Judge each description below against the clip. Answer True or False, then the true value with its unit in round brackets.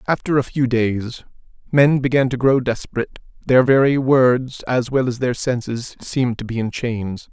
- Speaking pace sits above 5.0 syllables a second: False (4.7 syllables/s)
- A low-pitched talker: True (125 Hz)